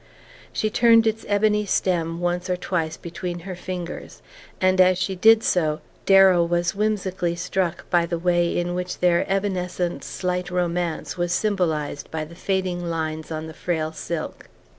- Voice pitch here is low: No, medium, 180 Hz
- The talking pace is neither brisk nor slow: Yes, average, 160 wpm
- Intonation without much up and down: Yes, narrow, 1.8 semitones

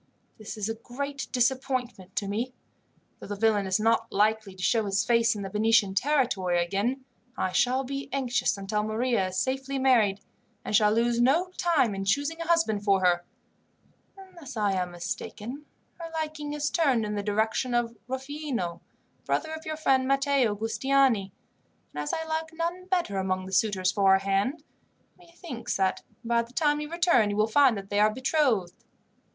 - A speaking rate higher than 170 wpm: Yes, average, 180 wpm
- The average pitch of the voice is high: Yes, high, 235 Hz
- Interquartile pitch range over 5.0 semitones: Yes, wide, 5.4 semitones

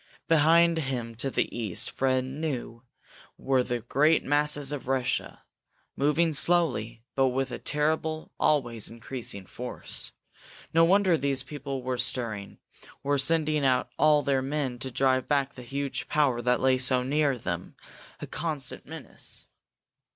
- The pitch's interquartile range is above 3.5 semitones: No, average, 3.0 semitones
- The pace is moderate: Yes, average, 145 wpm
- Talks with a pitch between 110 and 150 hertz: Yes, low, 135 Hz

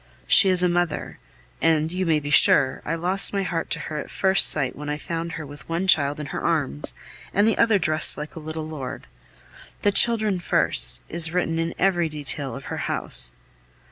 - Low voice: No, medium, 160 Hz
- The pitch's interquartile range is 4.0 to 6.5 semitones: No, average, 3.4 semitones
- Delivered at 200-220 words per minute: Yes, fast, 205 wpm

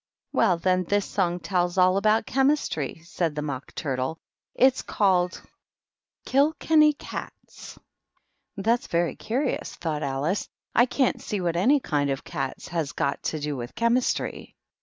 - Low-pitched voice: No, medium, 180 Hz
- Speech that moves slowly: No, average, 165 wpm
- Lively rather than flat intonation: Yes, wide, 7.4 semitones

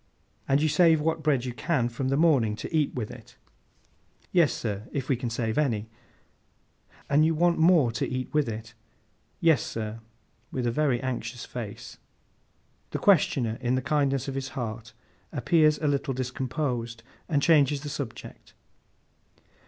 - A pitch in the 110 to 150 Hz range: Yes, low, 135 Hz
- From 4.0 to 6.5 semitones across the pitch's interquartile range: Yes, average, 4.3 semitones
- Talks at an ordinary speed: Yes, average, 155 wpm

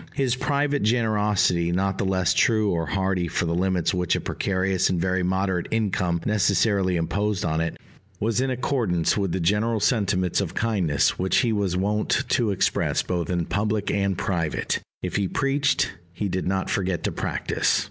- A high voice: No, very low, 95 Hz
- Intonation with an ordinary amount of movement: Yes, average, 3.0 semitones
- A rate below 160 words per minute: No, average, 175 wpm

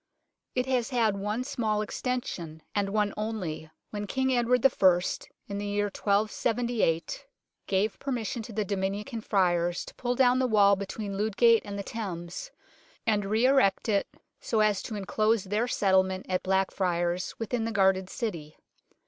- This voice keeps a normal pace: Yes, average, 165 wpm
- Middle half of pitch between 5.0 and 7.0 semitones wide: No, average, 3.2 semitones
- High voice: Yes, high, 210 Hz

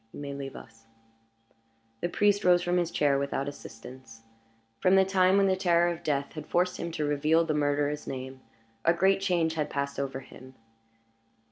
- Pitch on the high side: No, medium, 150 Hz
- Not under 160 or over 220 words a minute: Yes, average, 180 wpm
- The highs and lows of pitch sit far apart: No, average, 4.1 semitones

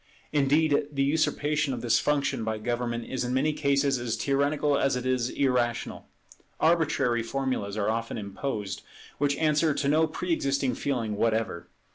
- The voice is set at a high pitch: No, low, 135 Hz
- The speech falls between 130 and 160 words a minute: Yes, average, 155 wpm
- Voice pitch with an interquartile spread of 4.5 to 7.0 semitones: No, average, 3.6 semitones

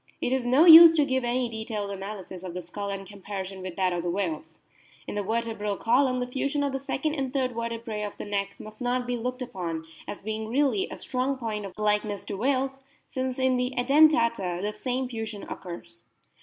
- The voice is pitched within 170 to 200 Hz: No, high, 230 Hz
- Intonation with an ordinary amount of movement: Yes, average, 4.5 semitones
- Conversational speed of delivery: No, fast, 210 wpm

